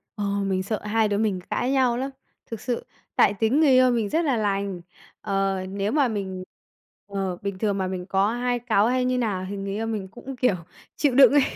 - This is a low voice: No, high, 215 Hz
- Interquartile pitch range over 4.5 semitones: No, average, 4.0 semitones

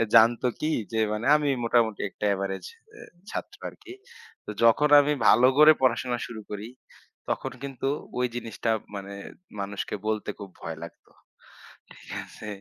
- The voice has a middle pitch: No, low, 115 Hz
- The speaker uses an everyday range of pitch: Yes, average, 4.6 semitones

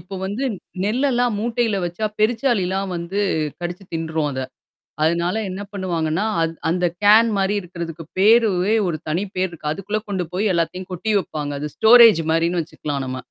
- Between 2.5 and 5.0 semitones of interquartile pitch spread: Yes, average, 4.3 semitones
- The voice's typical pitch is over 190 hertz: No, medium, 185 Hz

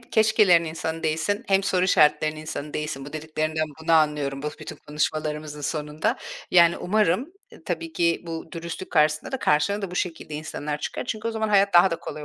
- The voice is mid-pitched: Yes, medium, 160 Hz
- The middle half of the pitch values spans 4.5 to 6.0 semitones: No, average, 3.8 semitones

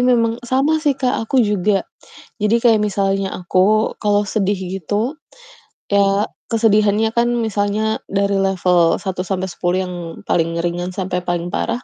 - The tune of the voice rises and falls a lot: No, average, 3.2 semitones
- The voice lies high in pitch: Yes, high, 205 Hz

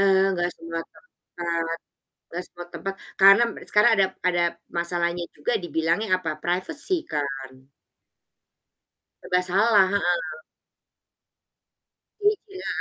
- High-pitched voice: No, medium, 175 Hz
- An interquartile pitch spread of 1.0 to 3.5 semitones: Yes, average, 2.9 semitones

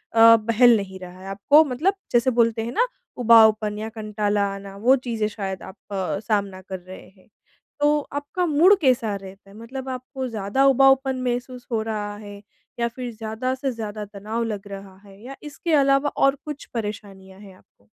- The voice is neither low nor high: No, high, 225 Hz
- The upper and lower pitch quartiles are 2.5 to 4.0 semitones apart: No, average, 4.4 semitones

